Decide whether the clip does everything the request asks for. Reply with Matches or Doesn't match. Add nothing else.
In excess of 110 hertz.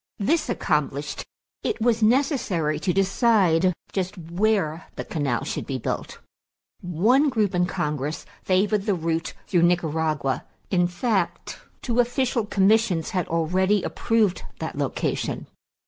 Matches